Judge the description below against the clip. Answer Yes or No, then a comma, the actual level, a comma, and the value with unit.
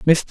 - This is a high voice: No, medium, 160 Hz